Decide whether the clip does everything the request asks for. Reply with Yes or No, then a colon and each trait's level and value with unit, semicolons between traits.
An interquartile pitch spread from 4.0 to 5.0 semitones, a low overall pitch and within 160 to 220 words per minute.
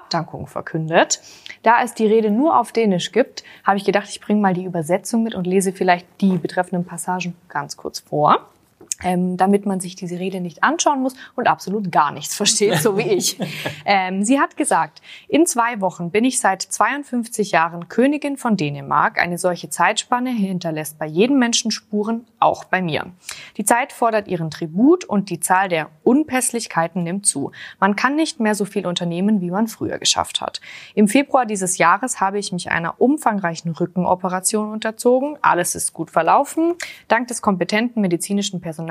No: average, 4.5 semitones; high, 200 Hz; average, 175 wpm